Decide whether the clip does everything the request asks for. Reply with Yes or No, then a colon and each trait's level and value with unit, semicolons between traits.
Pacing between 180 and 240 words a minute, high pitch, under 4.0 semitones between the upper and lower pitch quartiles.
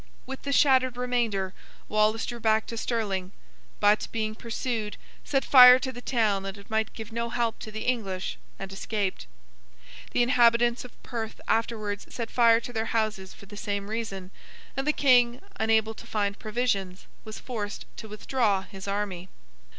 No: average, 165 wpm; high, 220 Hz; average, 2.8 semitones